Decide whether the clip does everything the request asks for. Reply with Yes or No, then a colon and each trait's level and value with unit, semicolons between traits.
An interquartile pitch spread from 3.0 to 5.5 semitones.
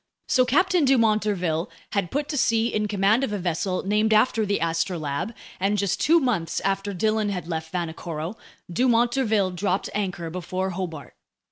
Yes: average, 4.1 semitones